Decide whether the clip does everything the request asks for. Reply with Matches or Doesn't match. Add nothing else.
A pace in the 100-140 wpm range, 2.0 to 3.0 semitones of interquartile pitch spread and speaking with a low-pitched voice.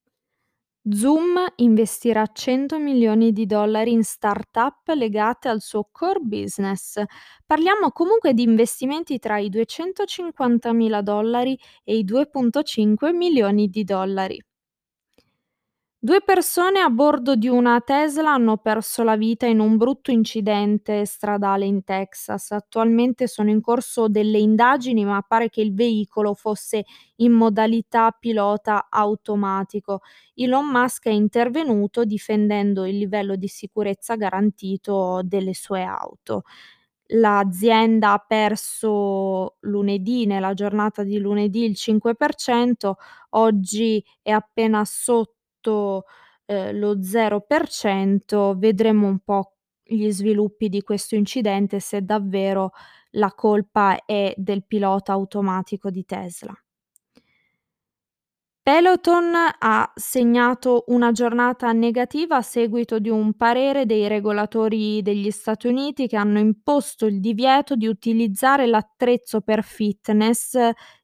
Doesn't match